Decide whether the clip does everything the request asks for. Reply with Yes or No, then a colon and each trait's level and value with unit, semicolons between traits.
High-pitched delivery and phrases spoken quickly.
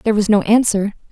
Yes: high, 210 Hz; fast, 215 wpm